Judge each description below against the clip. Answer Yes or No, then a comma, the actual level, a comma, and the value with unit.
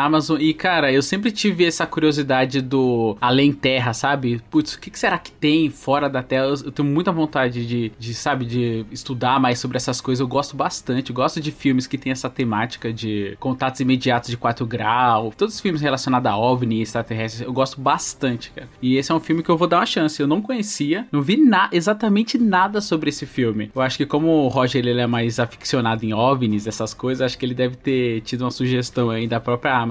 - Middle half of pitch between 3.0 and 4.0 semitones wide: Yes, average, 3.7 semitones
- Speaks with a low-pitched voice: Yes, low, 130 Hz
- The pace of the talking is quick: Yes, fast, 225 wpm